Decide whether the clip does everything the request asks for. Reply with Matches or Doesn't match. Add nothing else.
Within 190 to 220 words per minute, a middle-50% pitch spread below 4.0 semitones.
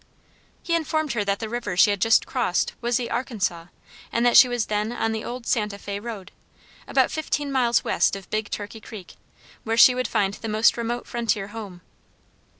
Matches